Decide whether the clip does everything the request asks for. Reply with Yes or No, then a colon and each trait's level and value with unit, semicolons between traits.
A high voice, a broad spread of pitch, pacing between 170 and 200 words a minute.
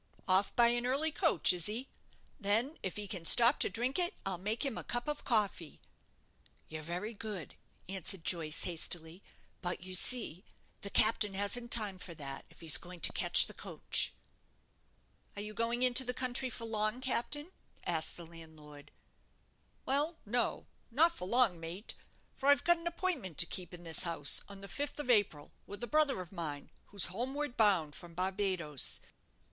Yes: high, 205 Hz; wide, 6.1 semitones; average, 175 wpm